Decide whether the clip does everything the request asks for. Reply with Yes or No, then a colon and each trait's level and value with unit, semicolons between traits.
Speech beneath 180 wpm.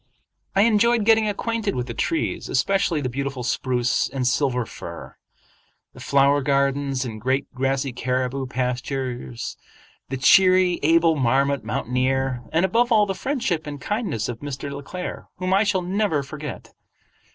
Yes: average, 150 wpm